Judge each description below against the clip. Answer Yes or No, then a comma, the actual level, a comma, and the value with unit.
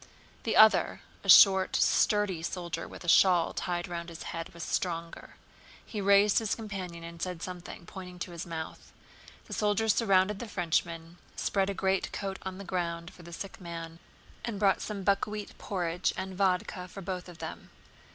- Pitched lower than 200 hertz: Yes, medium, 185 Hz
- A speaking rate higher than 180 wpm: No, average, 170 wpm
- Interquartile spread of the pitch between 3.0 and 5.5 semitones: No, narrow, 2.6 semitones